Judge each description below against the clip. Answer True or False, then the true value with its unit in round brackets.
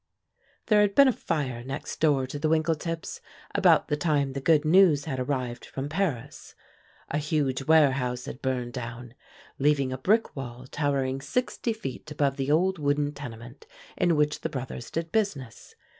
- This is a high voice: False (145 Hz)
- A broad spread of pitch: False (3.6 semitones)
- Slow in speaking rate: False (165 wpm)